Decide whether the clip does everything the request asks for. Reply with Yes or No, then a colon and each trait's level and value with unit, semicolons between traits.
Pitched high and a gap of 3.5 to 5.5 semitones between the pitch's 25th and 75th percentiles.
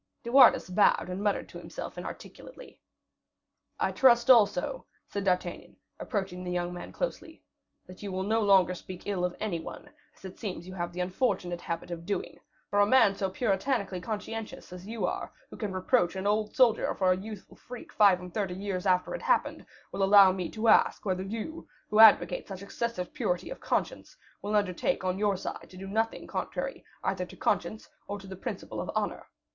No: high, 195 Hz; average, 2.9 semitones